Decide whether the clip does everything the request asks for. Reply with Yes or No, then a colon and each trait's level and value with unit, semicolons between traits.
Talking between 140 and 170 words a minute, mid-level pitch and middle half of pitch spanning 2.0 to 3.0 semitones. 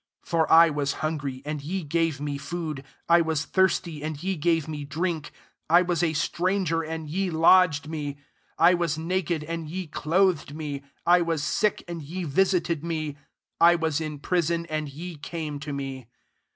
No: average, 185 wpm; medium, 160 Hz; narrow, 2.6 semitones